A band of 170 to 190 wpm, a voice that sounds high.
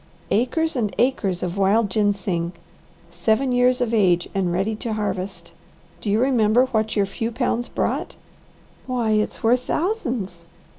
No: average, 145 wpm; high, 220 Hz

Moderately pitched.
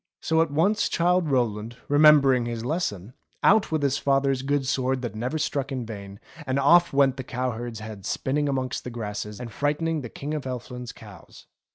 No: low, 130 Hz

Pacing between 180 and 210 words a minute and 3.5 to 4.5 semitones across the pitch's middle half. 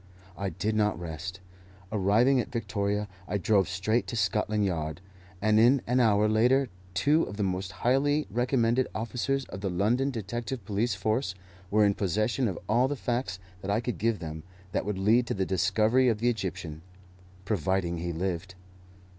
No: average, 170 wpm; average, 3.9 semitones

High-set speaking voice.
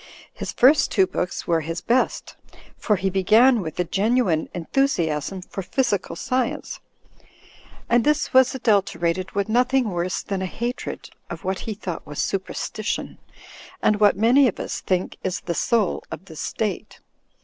Yes: high, 200 Hz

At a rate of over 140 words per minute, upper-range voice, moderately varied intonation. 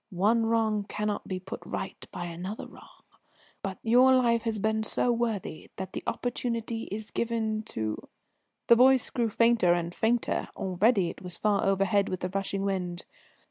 Yes: average, 170 wpm; high, 210 Hz; average, 3.5 semitones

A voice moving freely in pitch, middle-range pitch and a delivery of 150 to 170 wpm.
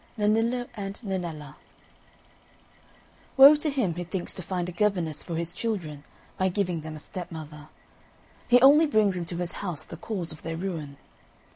No: average, 4.4 semitones; medium, 180 Hz; average, 165 wpm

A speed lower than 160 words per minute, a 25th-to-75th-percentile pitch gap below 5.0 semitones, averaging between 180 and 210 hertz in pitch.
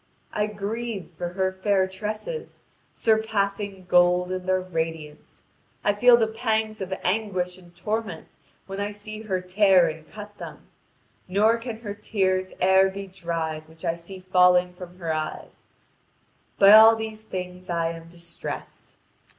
Yes: average, 150 wpm; average, 3.0 semitones; high, 190 Hz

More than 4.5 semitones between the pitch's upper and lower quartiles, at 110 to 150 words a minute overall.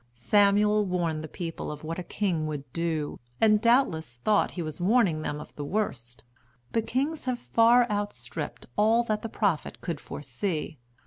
No: wide, 5.6 semitones; average, 170 wpm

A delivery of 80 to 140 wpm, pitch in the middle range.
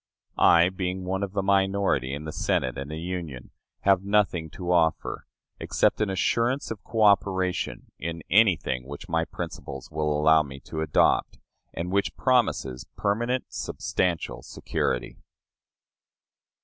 No: slow, 135 wpm; very low, 90 Hz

